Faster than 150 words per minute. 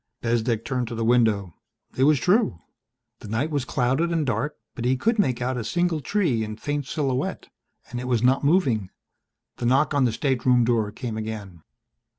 Yes: average, 185 wpm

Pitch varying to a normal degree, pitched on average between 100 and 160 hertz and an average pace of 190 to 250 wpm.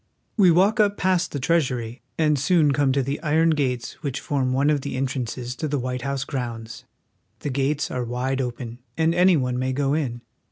Yes: average, 3.5 semitones; low, 135 Hz; average, 200 wpm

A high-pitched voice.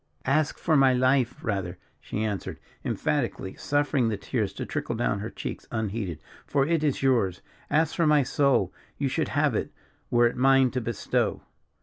No: low, 125 Hz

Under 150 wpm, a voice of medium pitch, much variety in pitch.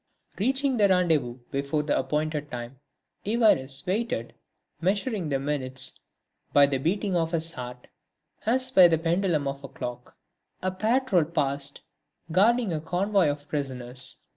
Yes: average, 140 wpm; medium, 160 Hz; wide, 6.0 semitones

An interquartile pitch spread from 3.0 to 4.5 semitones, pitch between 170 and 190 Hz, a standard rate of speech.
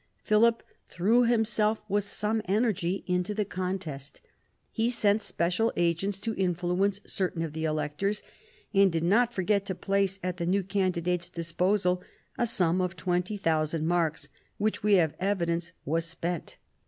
Yes: average, 3.4 semitones; medium, 185 Hz; average, 145 wpm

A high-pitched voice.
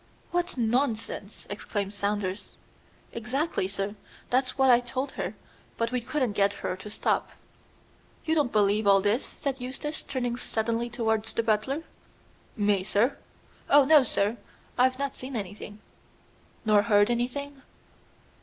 Yes: high, 230 Hz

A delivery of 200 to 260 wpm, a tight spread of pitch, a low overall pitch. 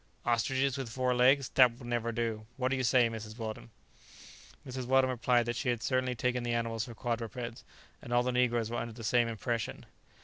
Yes: fast, 205 wpm; narrow, 1.6 semitones; low, 120 Hz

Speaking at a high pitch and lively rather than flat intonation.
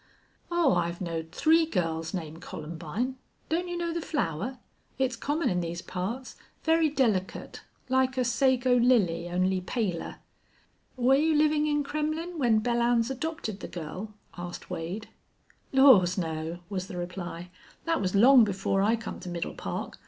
Yes: high, 225 Hz; wide, 7.5 semitones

